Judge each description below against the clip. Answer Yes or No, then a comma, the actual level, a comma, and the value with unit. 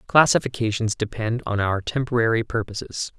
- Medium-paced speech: No, slow, 115 wpm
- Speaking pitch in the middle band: No, low, 115 Hz